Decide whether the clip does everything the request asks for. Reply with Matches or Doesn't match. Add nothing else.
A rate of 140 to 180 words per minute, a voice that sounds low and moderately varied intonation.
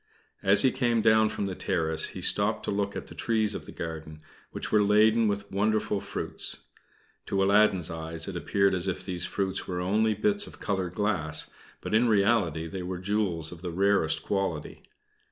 Doesn't match